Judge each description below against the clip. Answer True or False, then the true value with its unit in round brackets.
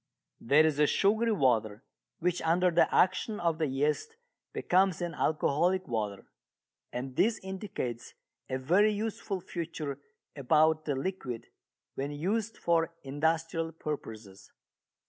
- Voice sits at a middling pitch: True (160 Hz)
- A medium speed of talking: False (125 wpm)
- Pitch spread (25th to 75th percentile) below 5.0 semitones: False (5.3 semitones)